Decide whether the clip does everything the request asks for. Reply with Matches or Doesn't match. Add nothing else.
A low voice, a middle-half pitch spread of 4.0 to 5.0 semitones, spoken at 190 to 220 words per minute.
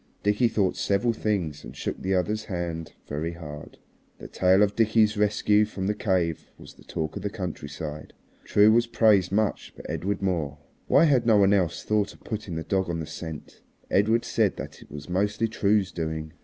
Matches